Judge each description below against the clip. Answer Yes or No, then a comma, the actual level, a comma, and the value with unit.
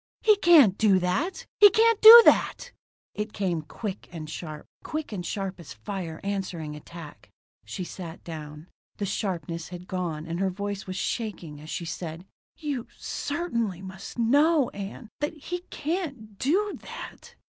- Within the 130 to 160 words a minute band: Yes, average, 155 wpm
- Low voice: No, high, 195 Hz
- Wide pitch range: Yes, wide, 8.7 semitones